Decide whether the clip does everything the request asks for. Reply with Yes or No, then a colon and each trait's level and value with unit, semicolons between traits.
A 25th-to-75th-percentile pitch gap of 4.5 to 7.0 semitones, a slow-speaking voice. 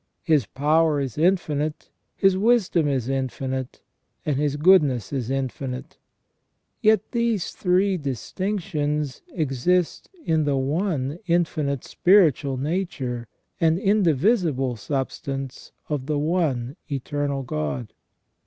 Yes: average, 5.0 semitones; slow, 105 wpm